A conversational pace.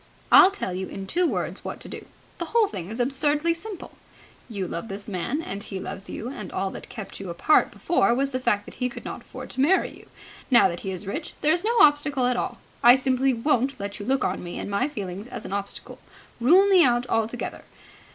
No: fast, 230 wpm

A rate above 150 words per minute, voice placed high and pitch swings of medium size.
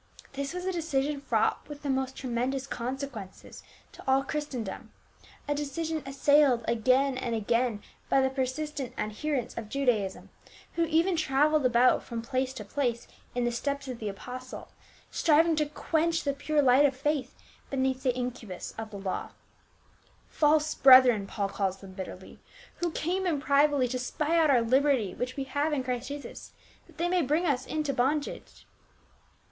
Yes: average, 170 wpm; very high, 270 Hz; average, 3.4 semitones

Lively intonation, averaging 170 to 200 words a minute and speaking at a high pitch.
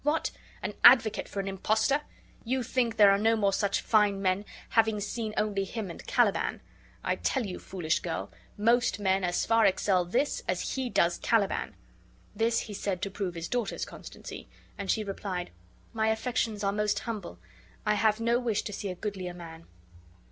No: average, 2.7 semitones; average, 180 wpm; high, 210 Hz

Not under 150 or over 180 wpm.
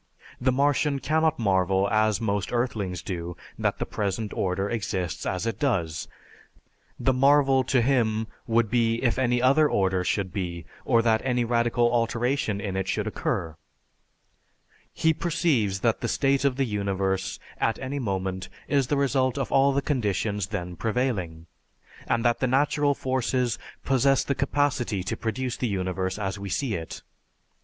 Yes: average, 160 wpm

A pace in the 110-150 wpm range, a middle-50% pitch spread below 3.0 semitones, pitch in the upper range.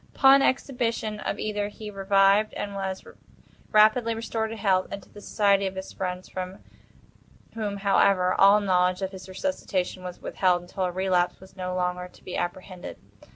No: average, 165 wpm; narrow, 2.4 semitones; high, 195 Hz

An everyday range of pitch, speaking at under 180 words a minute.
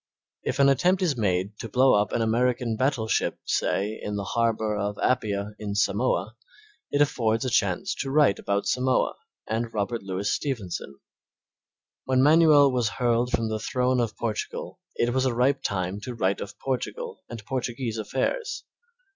Yes: average, 3.9 semitones; average, 165 wpm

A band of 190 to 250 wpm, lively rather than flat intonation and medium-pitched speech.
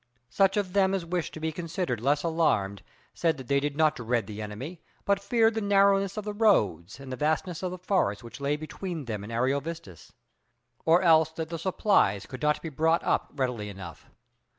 Yes: average, 200 wpm; wide, 6.6 semitones; medium, 160 Hz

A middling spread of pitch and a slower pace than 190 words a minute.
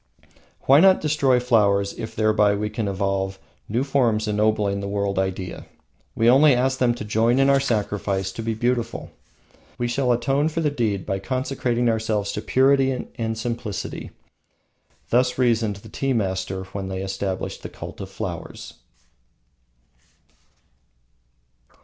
Yes: average, 4.1 semitones; average, 145 wpm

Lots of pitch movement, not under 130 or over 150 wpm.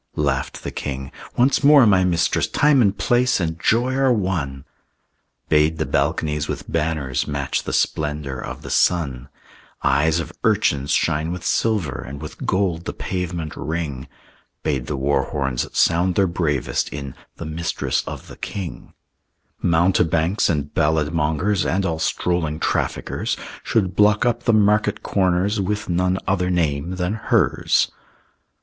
No: average, 4.4 semitones; average, 145 wpm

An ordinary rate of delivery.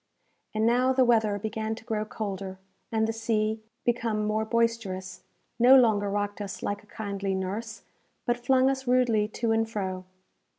Yes: average, 165 wpm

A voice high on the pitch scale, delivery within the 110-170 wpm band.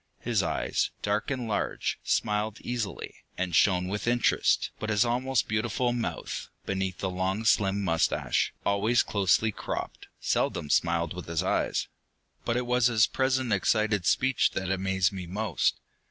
No: low, 105 Hz; average, 150 wpm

